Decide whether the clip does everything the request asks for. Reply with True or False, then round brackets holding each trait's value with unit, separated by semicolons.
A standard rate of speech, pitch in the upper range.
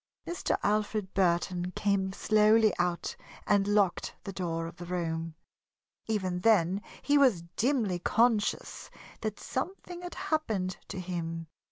False (130 wpm; 195 Hz)